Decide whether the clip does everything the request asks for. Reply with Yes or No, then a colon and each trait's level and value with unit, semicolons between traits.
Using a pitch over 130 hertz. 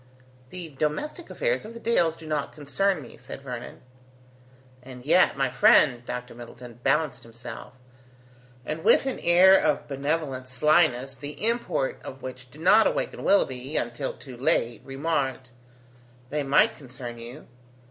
Yes: medium, 140 Hz